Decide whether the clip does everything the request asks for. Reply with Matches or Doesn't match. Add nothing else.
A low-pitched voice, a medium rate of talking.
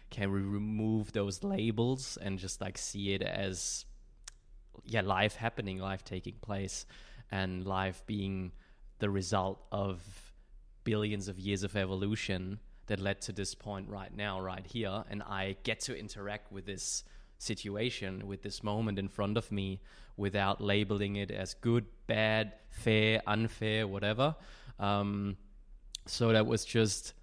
Matches